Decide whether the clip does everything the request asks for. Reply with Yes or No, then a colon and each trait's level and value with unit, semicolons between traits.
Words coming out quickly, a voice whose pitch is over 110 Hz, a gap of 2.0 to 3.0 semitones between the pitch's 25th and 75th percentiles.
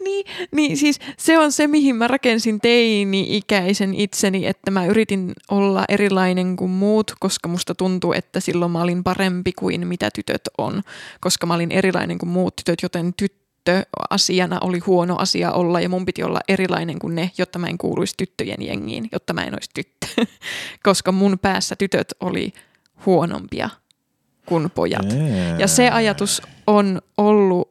Yes: fast, 160 wpm; high, 190 Hz; narrow, 2.5 semitones